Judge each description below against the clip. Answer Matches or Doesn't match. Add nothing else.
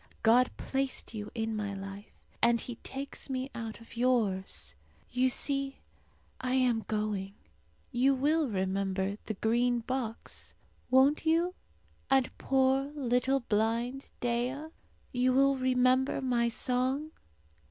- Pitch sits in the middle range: Doesn't match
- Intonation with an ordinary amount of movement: Matches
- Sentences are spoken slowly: Matches